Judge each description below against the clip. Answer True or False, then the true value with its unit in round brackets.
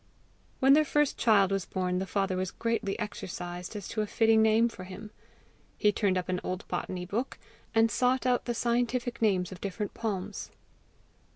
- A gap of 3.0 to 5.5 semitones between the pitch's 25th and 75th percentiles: True (3.8 semitones)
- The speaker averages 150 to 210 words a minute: True (180 wpm)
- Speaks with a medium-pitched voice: False (210 Hz)